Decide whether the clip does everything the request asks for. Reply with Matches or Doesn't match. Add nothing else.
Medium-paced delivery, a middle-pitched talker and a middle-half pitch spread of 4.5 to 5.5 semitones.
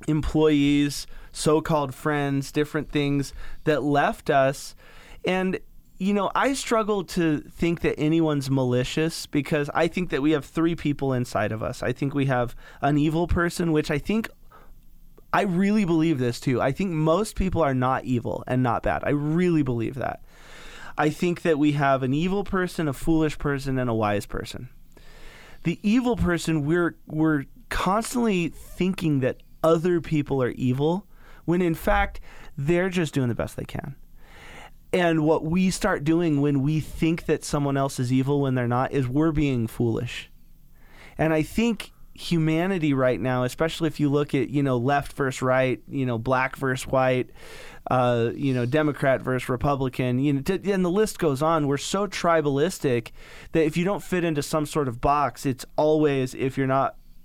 Doesn't match